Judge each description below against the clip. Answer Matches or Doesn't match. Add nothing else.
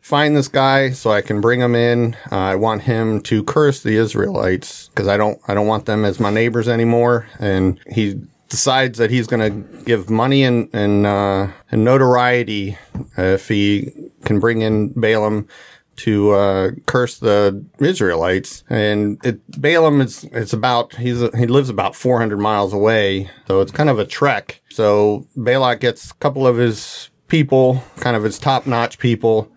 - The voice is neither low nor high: Doesn't match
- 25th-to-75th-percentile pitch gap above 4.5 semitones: Doesn't match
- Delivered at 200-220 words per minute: Doesn't match